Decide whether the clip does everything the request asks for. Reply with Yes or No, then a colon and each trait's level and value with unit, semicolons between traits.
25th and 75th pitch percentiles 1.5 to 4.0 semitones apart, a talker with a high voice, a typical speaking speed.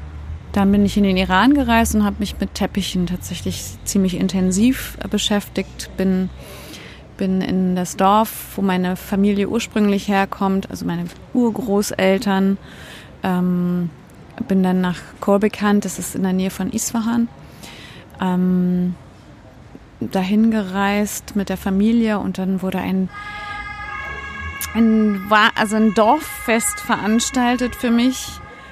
No: average, 2.7 semitones; high, 200 Hz; slow, 120 wpm